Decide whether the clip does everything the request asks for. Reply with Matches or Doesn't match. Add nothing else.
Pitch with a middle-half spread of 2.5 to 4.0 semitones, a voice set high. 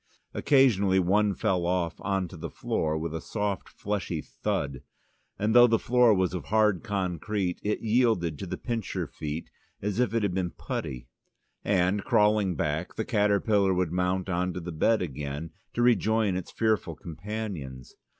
Doesn't match